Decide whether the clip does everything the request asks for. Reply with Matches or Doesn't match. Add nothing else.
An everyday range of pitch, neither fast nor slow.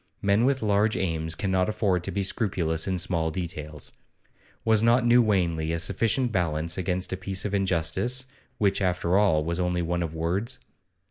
Matches